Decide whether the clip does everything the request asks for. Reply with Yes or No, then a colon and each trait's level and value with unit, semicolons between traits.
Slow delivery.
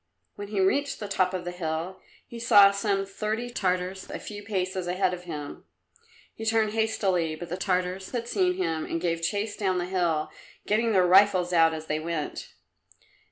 No: average, 185 wpm